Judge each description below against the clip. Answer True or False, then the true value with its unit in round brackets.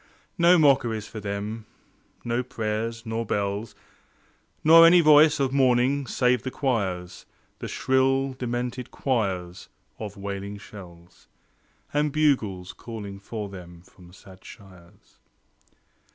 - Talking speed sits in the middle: False (115 wpm)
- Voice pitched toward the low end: True (115 Hz)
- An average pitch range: True (5.0 semitones)